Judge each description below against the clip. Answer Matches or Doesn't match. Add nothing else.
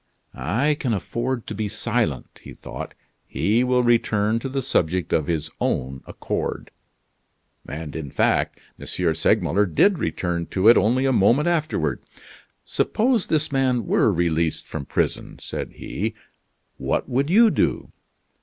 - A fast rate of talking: Doesn't match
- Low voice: Matches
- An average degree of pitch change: Doesn't match